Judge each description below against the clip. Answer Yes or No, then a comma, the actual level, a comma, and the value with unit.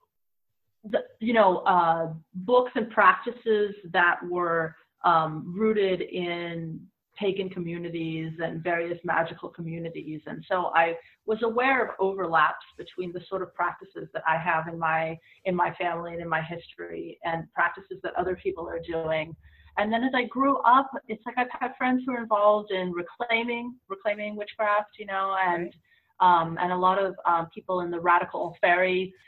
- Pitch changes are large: No, average, 4.2 semitones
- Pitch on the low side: No, medium, 185 Hz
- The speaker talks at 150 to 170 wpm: Yes, average, 165 wpm